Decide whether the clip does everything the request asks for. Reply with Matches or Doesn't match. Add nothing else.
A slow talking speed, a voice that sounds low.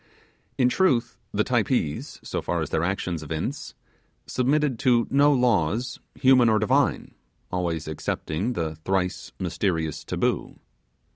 Matches